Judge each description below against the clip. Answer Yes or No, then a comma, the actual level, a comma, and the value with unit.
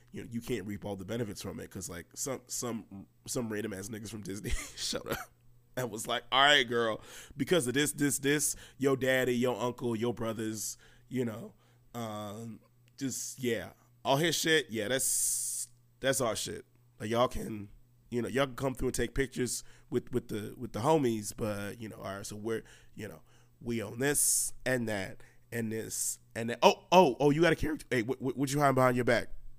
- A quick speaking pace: Yes, fast, 215 wpm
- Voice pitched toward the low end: Yes, low, 120 Hz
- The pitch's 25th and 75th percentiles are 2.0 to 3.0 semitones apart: Yes, narrow, 2.4 semitones